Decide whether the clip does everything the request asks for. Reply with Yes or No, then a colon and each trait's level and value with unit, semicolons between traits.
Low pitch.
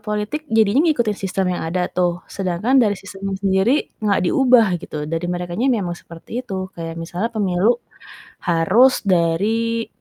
No: high, 195 Hz